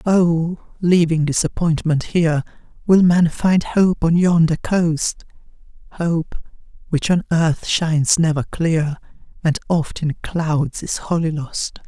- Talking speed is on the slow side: Yes, slow, 125 wpm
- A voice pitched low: No, medium, 165 Hz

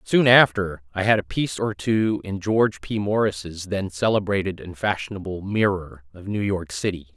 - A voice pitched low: Yes, very low, 95 Hz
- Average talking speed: Yes, average, 175 wpm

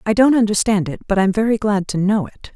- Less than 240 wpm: No, fast, 260 wpm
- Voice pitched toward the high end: Yes, high, 205 Hz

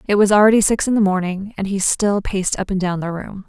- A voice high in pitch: Yes, high, 195 Hz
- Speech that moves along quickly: Yes, fast, 275 wpm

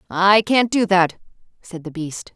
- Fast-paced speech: No, average, 180 wpm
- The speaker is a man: No, female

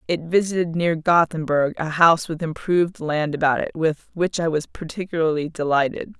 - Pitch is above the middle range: No, medium, 160 Hz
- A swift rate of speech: No, average, 165 wpm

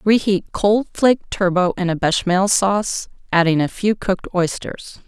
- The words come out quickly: No, average, 155 wpm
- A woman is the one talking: Yes, female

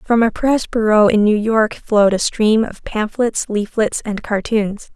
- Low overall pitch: No, high, 215 Hz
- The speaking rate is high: No, average, 180 wpm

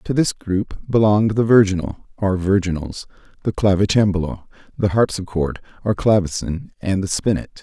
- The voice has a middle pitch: No, low, 100 Hz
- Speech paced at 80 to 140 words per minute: Yes, slow, 135 wpm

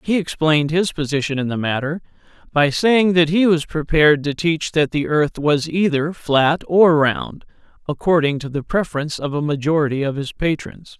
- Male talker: Yes, male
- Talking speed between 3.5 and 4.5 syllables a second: No, 5.0 syllables/s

